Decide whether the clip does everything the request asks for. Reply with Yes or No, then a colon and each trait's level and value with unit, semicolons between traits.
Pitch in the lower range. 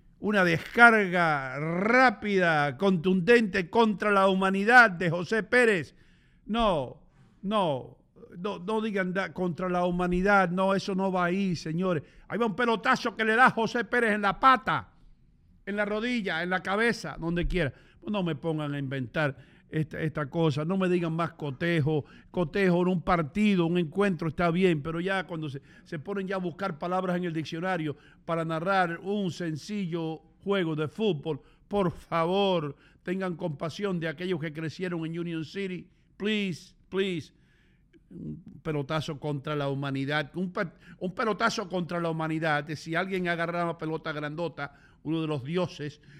No: medium, 180 Hz